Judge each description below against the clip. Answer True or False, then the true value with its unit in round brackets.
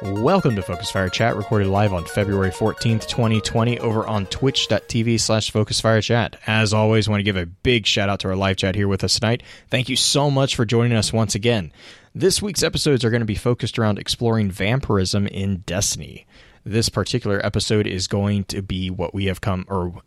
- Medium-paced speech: False (210 wpm)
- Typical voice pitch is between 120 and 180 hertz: False (110 Hz)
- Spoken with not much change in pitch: False (3.0 semitones)